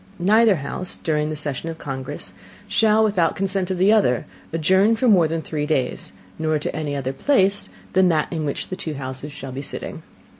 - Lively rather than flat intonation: No, average, 4.6 semitones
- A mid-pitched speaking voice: Yes, medium, 160 Hz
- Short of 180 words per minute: No, average, 200 wpm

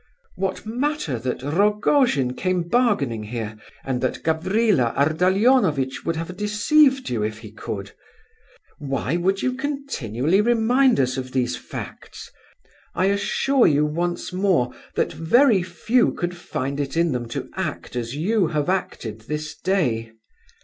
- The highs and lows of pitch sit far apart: Yes, wide, 8.3 semitones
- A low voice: No, medium, 170 Hz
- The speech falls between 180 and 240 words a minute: No, average, 140 wpm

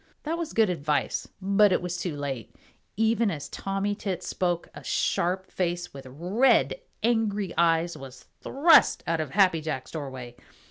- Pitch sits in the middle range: Yes, medium, 175 Hz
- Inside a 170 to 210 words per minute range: No, average, 155 wpm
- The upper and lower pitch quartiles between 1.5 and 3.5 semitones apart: No, average, 4.9 semitones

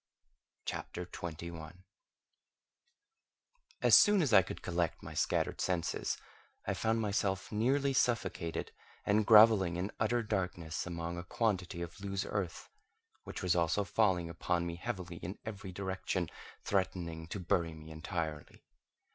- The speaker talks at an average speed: No, slow, 130 wpm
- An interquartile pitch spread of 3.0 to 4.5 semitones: Yes, average, 3.4 semitones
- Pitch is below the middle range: Yes, very low, 90 Hz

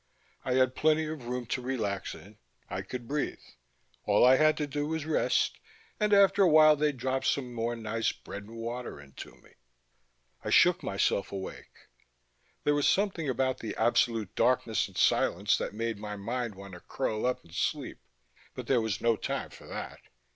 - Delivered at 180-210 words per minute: Yes, average, 185 wpm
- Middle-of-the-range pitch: No, low, 125 Hz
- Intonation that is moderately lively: Yes, average, 5.0 semitones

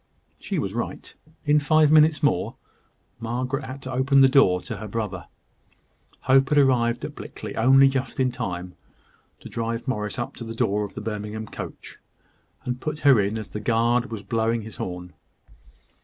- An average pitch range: Yes, average, 4.0 semitones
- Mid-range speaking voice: No, low, 120 Hz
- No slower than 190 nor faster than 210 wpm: No, average, 175 wpm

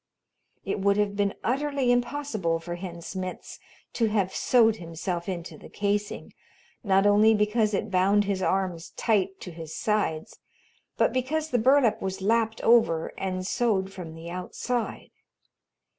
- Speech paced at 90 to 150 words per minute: Yes, average, 145 wpm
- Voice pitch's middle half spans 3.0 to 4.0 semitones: Yes, average, 3.5 semitones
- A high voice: Yes, high, 200 Hz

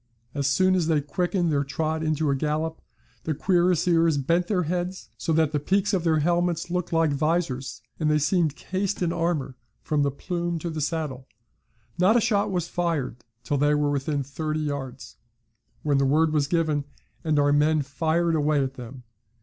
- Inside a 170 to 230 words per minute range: Yes, average, 185 wpm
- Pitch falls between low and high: Yes, medium, 155 Hz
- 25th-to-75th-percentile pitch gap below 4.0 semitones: Yes, average, 3.2 semitones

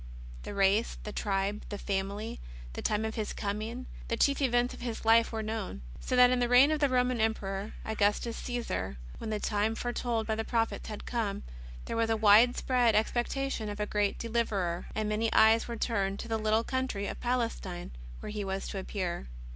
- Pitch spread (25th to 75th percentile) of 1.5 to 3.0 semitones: Yes, narrow, 2.6 semitones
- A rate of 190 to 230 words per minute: Yes, average, 195 wpm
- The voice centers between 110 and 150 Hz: No, high, 220 Hz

